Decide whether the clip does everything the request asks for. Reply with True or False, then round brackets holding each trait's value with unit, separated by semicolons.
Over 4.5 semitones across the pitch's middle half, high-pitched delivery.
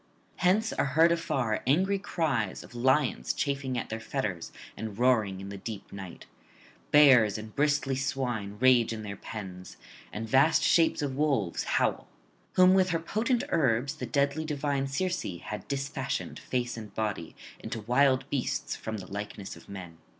False (5.3 semitones; 130 Hz)